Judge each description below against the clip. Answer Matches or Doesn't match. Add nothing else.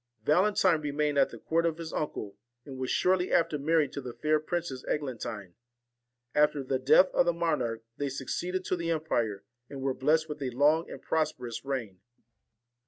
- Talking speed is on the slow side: Doesn't match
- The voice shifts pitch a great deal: Doesn't match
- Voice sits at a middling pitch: Matches